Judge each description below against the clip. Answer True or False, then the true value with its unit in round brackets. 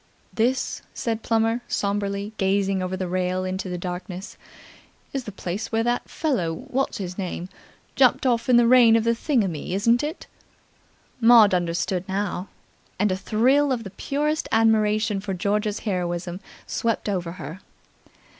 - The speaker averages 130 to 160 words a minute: True (145 wpm)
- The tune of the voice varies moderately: True (3.9 semitones)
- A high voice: True (205 Hz)